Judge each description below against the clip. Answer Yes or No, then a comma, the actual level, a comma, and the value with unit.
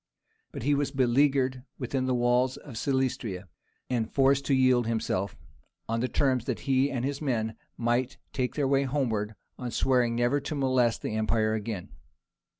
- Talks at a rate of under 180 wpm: Yes, average, 165 wpm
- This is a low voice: Yes, low, 125 Hz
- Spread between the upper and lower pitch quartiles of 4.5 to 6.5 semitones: No, average, 2.7 semitones